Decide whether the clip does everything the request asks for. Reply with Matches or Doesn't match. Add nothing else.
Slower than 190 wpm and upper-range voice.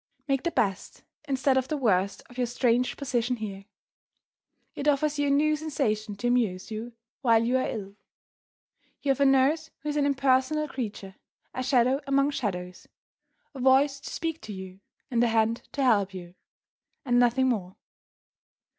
Matches